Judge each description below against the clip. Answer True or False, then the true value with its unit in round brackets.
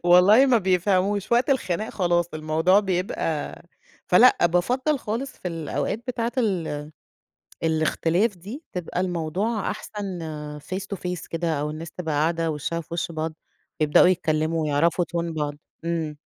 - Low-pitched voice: False (175 Hz)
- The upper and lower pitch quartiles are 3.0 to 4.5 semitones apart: True (3.9 semitones)